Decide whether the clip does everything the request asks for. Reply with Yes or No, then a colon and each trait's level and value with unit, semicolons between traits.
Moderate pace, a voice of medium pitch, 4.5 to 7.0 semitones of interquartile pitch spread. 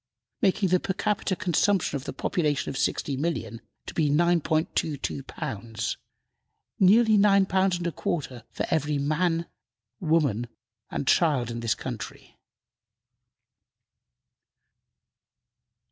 No: slow, 110 wpm; medium, 160 Hz; average, 5.3 semitones